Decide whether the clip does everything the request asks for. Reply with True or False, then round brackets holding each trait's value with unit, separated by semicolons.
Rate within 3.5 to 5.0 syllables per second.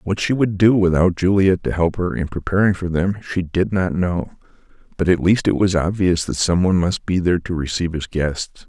False (5.3 syllables/s)